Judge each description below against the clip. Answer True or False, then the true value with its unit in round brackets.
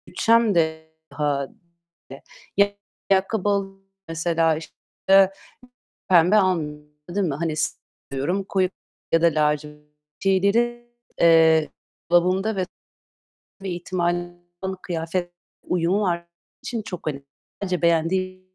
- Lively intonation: False (3.0 semitones)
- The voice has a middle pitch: True (175 Hz)